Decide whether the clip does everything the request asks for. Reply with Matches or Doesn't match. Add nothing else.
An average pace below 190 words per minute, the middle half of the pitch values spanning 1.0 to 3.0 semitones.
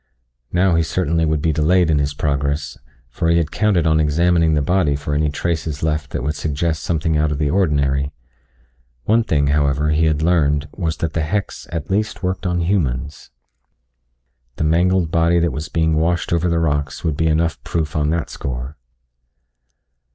Matches